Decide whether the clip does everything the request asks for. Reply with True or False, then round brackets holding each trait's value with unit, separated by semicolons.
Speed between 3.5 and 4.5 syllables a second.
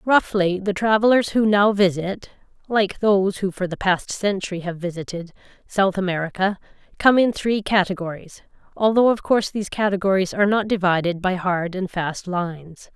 True (4.3 syllables/s)